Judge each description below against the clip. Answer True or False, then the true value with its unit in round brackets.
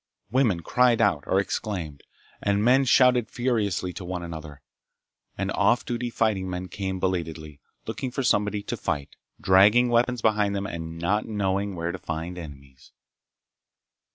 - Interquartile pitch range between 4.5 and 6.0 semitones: True (5.2 semitones)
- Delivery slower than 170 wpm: True (150 wpm)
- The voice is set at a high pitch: False (100 Hz)